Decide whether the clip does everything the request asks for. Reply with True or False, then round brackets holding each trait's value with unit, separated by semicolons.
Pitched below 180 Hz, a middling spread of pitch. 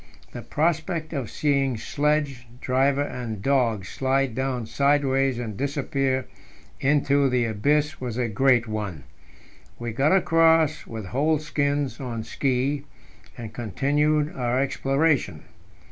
True (135 Hz; 3.3 semitones)